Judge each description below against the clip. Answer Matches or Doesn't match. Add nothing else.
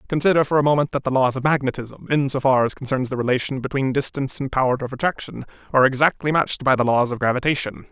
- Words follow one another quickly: Matches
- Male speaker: Matches